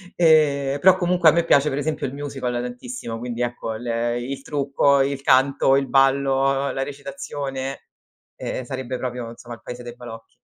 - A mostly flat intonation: Yes, narrow, 2.3 semitones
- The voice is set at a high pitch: No, low, 135 Hz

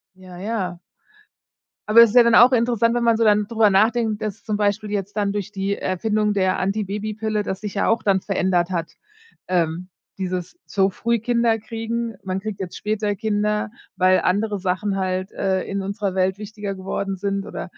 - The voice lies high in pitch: Yes, high, 205 Hz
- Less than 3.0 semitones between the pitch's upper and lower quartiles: Yes, narrow, 2.4 semitones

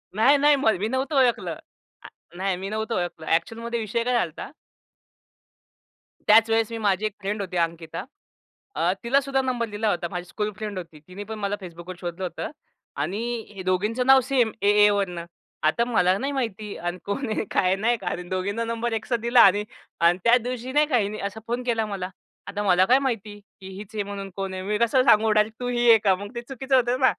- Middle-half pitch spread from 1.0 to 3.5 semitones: No, average, 3.9 semitones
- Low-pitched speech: No, high, 215 Hz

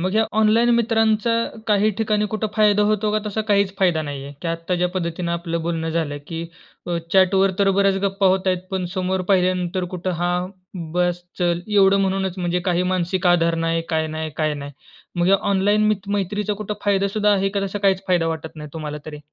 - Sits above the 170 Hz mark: Yes, medium, 185 Hz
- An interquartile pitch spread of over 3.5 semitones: No, average, 2.9 semitones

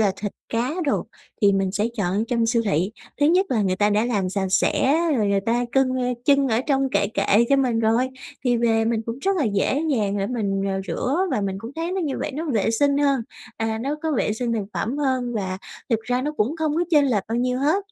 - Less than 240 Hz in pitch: Yes, high, 230 Hz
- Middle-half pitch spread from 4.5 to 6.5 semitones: Yes, average, 4.9 semitones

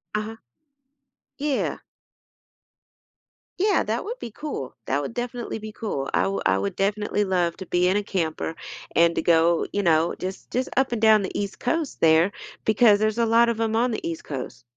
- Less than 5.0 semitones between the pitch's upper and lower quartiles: No, wide, 5.5 semitones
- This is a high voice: Yes, high, 205 Hz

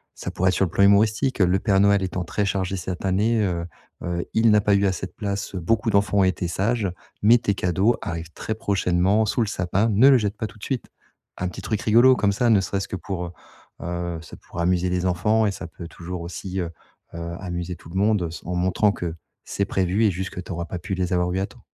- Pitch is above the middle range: No, very low, 95 Hz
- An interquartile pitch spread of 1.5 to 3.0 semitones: Yes, average, 2.7 semitones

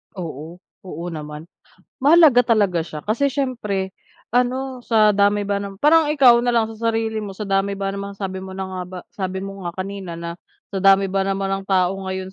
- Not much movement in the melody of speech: No, average, 3.2 semitones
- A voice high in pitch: Yes, high, 195 Hz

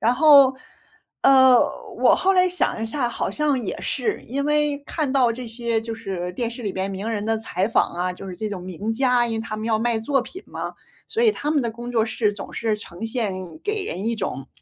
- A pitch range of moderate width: Yes, average, 4.2 semitones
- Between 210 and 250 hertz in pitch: Yes, high, 230 Hz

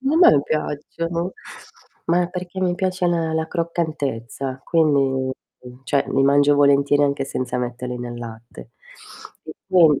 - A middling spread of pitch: Yes, average, 4.3 semitones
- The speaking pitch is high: No, medium, 145 Hz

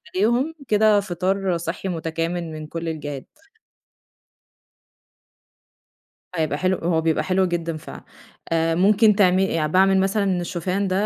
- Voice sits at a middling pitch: Yes, medium, 180 Hz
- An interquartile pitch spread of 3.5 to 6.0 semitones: No, average, 2.9 semitones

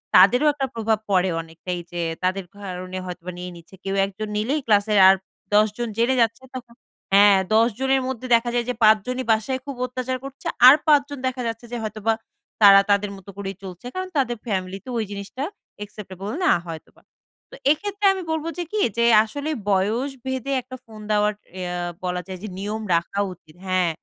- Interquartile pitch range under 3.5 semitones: No, average, 4.9 semitones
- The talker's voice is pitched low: No, high, 215 Hz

